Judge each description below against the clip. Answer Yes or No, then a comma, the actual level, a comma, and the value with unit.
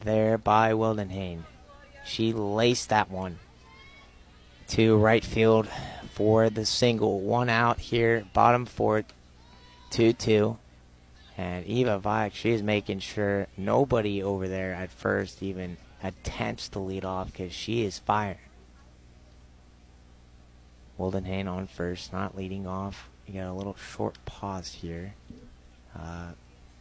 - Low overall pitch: Yes, very low, 95 Hz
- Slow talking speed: Yes, slow, 120 wpm